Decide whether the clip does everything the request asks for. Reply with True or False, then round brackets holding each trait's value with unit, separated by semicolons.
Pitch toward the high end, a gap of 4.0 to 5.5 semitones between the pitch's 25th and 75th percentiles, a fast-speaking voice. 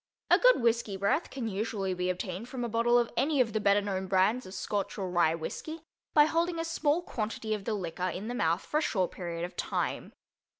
True (210 Hz; 4.9 semitones; 225 wpm)